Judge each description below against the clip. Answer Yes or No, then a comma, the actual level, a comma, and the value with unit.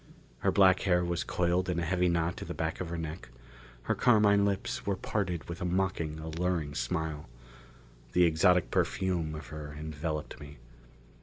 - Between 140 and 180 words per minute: Yes, average, 170 wpm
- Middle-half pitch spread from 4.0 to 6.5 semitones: No, average, 2.8 semitones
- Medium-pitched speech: No, very low, 85 Hz